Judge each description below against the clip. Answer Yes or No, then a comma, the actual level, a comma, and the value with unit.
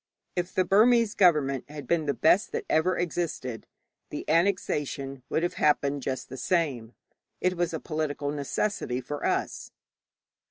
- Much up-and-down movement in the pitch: No, average, 4.2 semitones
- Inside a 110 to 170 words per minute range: Yes, average, 150 wpm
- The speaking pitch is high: No, medium, 155 Hz